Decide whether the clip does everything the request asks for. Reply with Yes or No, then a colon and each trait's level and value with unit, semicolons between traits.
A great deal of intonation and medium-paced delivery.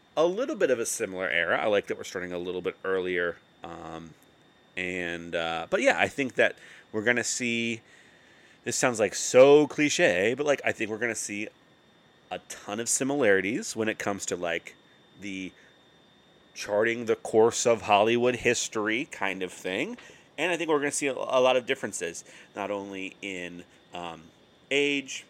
Yes: wide, 6.7 semitones; average, 175 wpm